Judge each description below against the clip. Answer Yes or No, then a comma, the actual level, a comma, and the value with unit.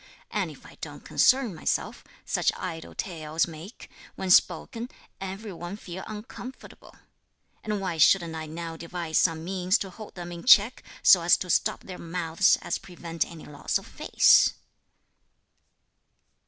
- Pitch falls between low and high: Yes, medium, 175 Hz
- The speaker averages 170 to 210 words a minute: No, average, 150 wpm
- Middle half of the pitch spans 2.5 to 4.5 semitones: Yes, average, 2.9 semitones